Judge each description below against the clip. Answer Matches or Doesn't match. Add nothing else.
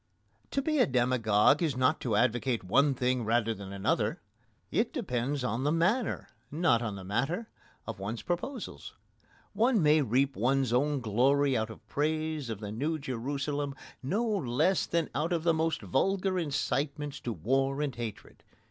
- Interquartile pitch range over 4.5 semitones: Matches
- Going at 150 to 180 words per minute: Matches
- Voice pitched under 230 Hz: Matches